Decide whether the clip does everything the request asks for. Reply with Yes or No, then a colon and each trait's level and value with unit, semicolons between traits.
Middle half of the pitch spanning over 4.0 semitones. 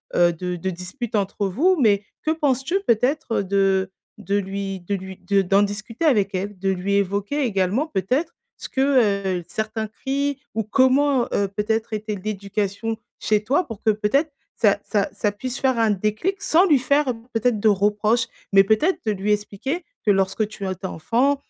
Yes: average, 4.6 semitones